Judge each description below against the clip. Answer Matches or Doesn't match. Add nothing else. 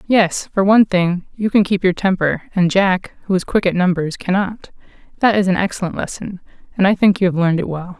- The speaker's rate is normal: Doesn't match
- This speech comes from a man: Doesn't match